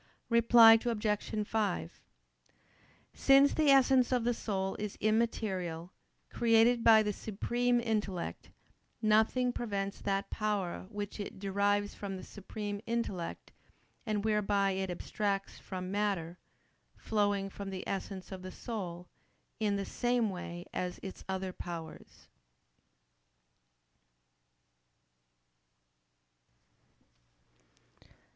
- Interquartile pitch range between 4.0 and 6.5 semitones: No, average, 2.8 semitones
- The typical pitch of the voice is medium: No, high, 205 Hz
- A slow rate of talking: Yes, slow, 100 wpm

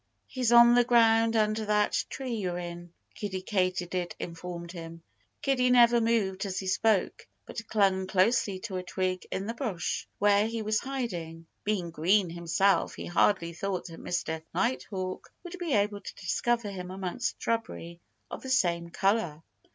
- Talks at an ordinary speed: Yes, average, 160 wpm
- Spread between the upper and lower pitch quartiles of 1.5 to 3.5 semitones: No, average, 4.3 semitones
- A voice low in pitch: No, high, 195 Hz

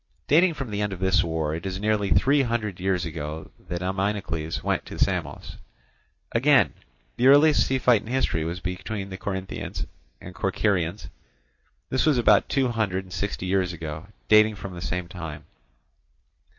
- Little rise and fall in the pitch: No, average, 3.8 semitones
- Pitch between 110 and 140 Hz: No, very low, 95 Hz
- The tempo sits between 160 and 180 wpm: Yes, average, 165 wpm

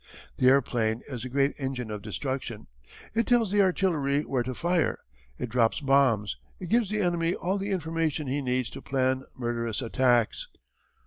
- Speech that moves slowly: No, average, 170 wpm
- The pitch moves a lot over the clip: Yes, wide, 5.7 semitones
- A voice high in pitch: No, low, 135 Hz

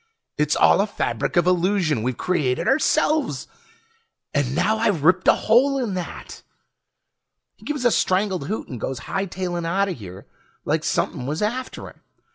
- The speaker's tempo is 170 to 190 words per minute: No, average, 155 wpm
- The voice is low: No, medium, 185 Hz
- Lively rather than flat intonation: Yes, wide, 7.1 semitones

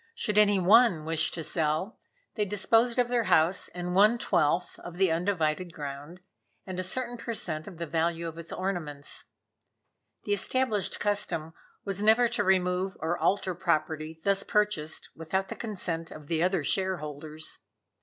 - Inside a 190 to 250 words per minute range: No, average, 160 wpm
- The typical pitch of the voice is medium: Yes, medium, 180 Hz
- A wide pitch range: No, average, 4.2 semitones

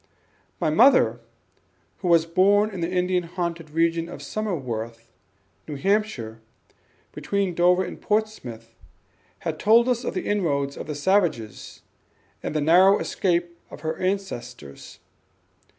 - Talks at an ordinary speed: No, slow, 125 wpm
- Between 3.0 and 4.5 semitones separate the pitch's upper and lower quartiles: No, average, 5.1 semitones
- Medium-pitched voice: Yes, medium, 175 Hz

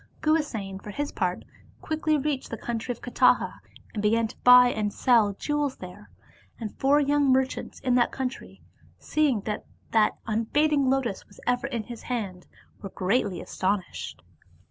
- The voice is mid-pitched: No, high, 240 Hz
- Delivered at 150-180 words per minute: Yes, average, 165 wpm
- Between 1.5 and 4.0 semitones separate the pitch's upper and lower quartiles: No, average, 4.7 semitones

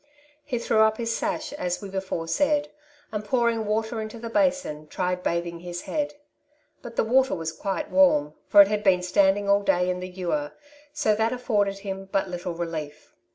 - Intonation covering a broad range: No, average, 4.5 semitones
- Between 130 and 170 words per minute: No, average, 190 wpm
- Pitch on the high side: Yes, high, 200 Hz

